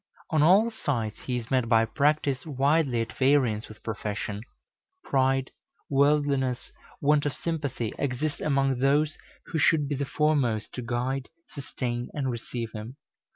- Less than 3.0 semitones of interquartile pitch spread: No, average, 3.4 semitones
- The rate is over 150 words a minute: No, average, 145 wpm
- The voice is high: No, low, 135 Hz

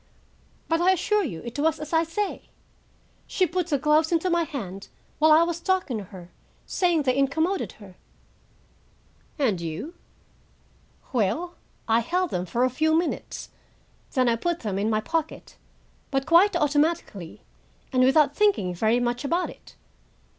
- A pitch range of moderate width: No, wide, 6.6 semitones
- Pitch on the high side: Yes, very high, 300 Hz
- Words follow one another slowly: No, average, 155 wpm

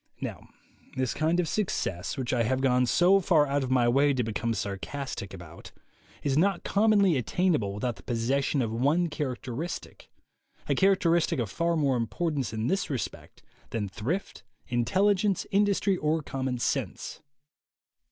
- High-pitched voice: No, low, 135 Hz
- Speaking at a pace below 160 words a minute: Yes, average, 150 wpm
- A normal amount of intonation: No, wide, 6.4 semitones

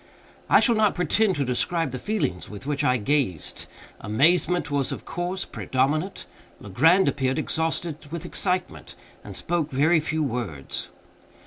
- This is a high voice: No, medium, 150 Hz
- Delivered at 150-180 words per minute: No, average, 140 wpm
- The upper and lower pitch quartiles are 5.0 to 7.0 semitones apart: Yes, wide, 5.4 semitones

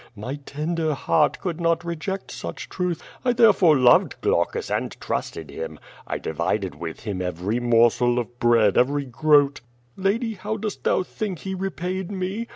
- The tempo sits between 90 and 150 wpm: No, average, 160 wpm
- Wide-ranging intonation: Yes, wide, 8.0 semitones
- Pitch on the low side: No, medium, 155 Hz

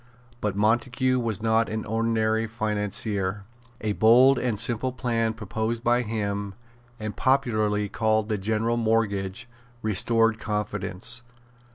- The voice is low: Yes, low, 110 Hz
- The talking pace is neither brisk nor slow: No, slow, 115 wpm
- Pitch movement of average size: No, narrow, 1.8 semitones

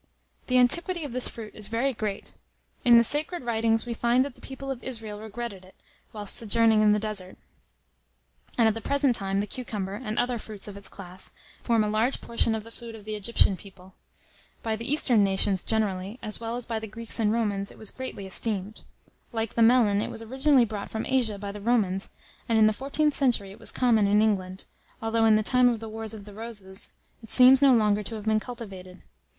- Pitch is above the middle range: Yes, high, 220 Hz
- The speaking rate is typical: No, fast, 220 wpm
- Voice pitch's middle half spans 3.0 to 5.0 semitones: No, narrow, 2.6 semitones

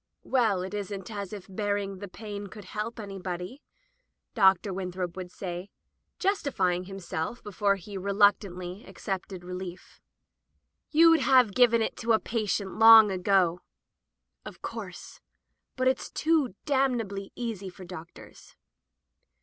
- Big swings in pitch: No, average, 3.4 semitones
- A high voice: Yes, high, 200 Hz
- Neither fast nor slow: No, slow, 125 wpm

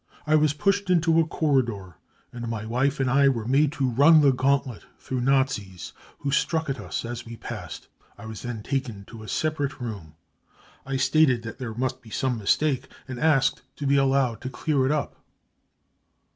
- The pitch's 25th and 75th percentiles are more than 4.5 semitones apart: No, average, 3.5 semitones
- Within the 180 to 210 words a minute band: Yes, average, 185 wpm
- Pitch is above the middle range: No, low, 130 Hz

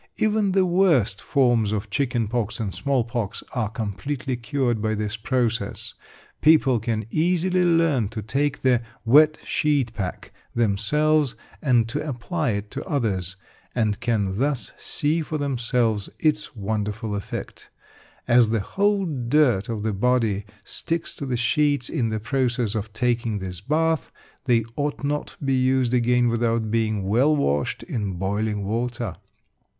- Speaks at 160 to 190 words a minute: No, average, 150 wpm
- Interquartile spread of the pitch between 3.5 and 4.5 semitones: No, average, 4.9 semitones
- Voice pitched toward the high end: No, low, 120 Hz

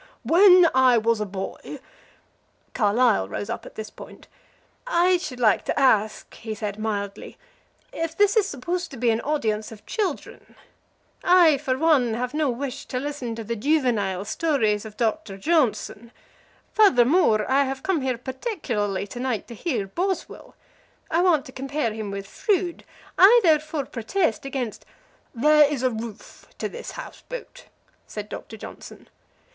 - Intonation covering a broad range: Yes, wide, 6.4 semitones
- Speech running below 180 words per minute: Yes, average, 160 wpm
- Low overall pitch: No, very high, 255 Hz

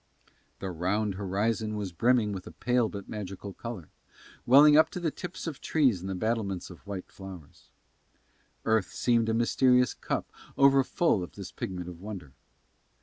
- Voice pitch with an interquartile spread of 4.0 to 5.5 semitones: Yes, average, 4.6 semitones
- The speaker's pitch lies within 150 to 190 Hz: No, low, 105 Hz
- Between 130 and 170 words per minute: Yes, average, 160 wpm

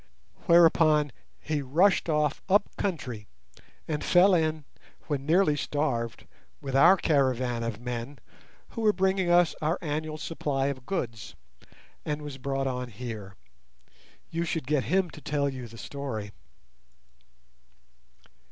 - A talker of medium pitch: Yes, medium, 145 Hz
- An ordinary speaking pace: No, slow, 130 wpm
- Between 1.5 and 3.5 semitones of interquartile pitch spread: No, average, 4.4 semitones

